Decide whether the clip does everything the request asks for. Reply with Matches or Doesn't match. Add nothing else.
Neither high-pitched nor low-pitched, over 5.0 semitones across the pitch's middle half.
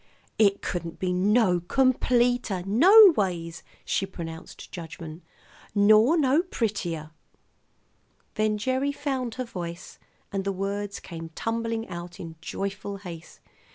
Doesn't match